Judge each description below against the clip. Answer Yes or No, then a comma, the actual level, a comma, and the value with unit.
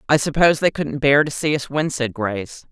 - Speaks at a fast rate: Yes, fast, 245 wpm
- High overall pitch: No, medium, 140 Hz